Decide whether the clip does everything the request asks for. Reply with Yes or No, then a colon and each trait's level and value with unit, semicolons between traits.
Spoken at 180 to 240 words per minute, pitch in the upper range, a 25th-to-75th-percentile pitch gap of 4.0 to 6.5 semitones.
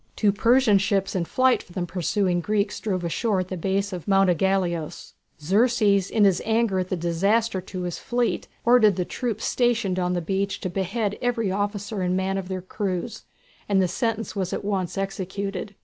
No: average, 190 wpm; high, 195 Hz; narrow, 2.6 semitones